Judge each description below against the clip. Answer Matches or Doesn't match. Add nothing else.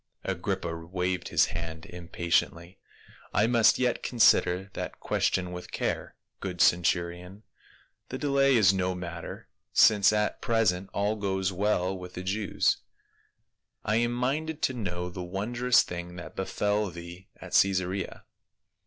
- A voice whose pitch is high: Doesn't match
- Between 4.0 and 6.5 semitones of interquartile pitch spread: Doesn't match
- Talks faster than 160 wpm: Doesn't match